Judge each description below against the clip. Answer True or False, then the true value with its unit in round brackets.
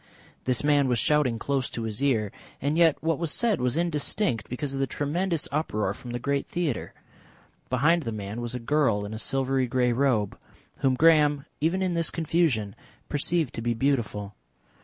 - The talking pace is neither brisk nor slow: True (180 wpm)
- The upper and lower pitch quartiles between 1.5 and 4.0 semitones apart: False (4.6 semitones)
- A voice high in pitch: False (135 Hz)